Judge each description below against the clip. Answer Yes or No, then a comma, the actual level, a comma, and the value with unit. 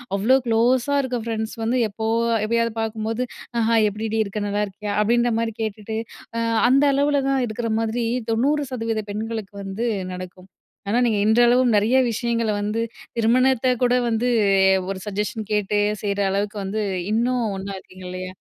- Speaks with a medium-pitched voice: No, high, 225 Hz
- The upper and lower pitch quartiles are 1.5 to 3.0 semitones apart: Yes, narrow, 2.5 semitones